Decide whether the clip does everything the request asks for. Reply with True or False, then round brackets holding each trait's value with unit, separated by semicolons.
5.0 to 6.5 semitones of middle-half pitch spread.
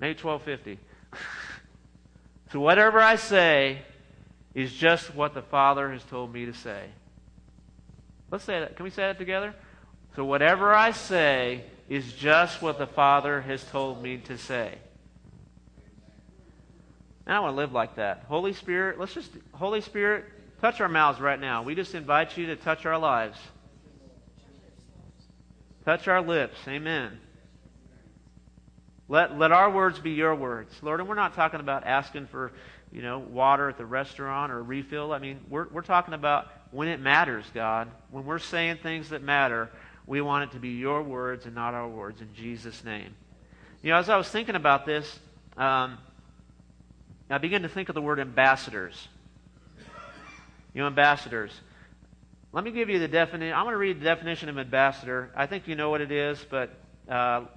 True (5.5 semitones)